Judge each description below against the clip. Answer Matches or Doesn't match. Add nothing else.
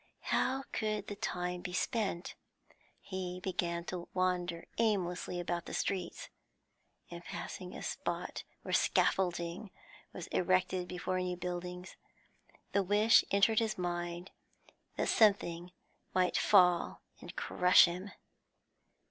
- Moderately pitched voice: Matches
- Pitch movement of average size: Doesn't match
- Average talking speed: Doesn't match